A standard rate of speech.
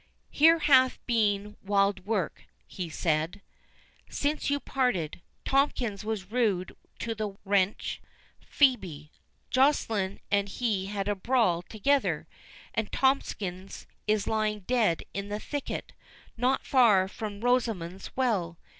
No: slow, 115 wpm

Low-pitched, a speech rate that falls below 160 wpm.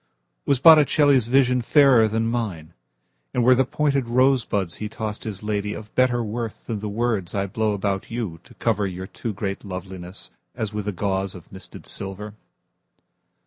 Yes: low, 105 Hz; slow, 135 wpm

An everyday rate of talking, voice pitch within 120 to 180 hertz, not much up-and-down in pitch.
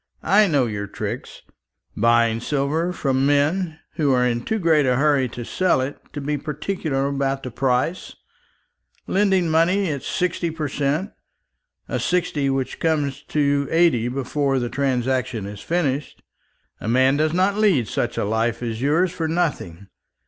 No: average, 155 wpm; medium, 140 Hz; average, 4.4 semitones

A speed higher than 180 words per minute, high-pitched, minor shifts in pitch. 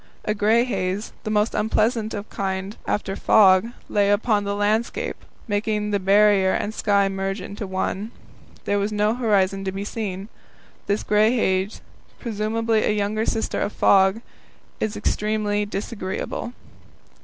No: average, 150 wpm; high, 210 Hz; narrow, 1.7 semitones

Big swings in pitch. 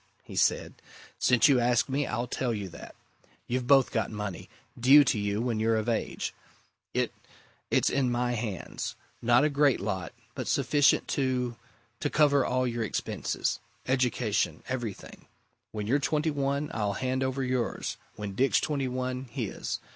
No: average, 3.2 semitones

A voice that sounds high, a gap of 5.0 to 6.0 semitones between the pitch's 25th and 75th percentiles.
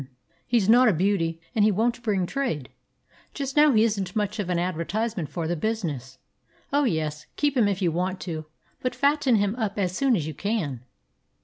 Yes: high, 200 Hz; wide, 5.6 semitones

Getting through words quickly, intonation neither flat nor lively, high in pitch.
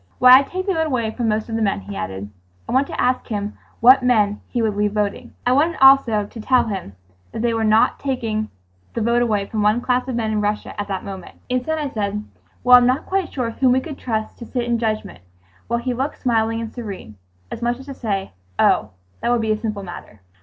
Yes: fast, 230 wpm; average, 3.3 semitones; high, 225 Hz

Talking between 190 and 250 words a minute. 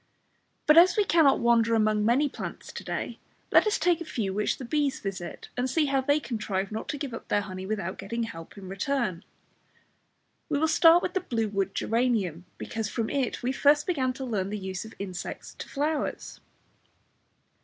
Yes: average, 195 wpm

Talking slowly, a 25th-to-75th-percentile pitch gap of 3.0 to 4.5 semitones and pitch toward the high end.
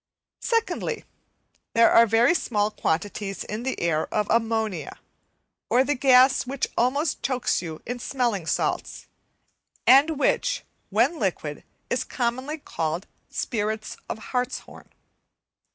Yes: slow, 105 wpm; average, 4.1 semitones; high, 235 Hz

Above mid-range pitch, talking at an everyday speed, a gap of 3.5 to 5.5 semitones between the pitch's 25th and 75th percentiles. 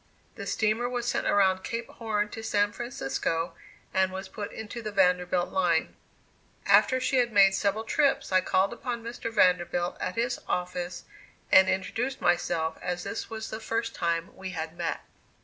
Yes: high, 195 Hz; average, 165 wpm; average, 4.1 semitones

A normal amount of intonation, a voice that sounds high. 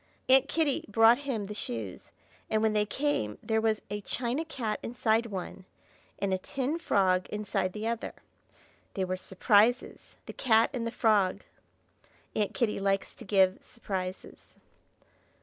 Yes: average, 3.4 semitones; high, 215 Hz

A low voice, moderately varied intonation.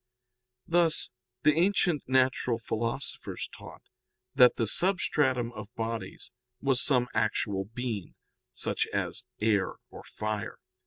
Yes: low, 125 Hz; average, 4.2 semitones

